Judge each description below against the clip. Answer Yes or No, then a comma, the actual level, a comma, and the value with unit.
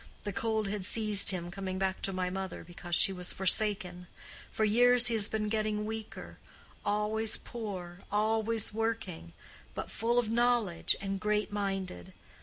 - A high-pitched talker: Yes, high, 210 Hz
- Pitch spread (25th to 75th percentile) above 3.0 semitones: No, average, 2.7 semitones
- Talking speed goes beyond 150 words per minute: No, average, 145 wpm